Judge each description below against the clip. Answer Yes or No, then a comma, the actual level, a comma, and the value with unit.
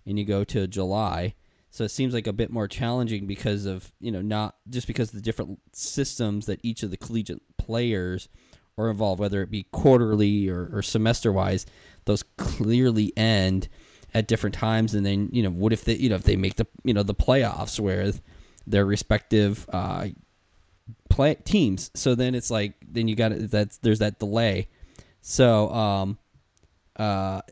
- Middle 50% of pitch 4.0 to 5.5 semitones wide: No, average, 2.7 semitones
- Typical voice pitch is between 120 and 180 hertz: No, low, 105 Hz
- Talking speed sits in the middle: Yes, average, 185 wpm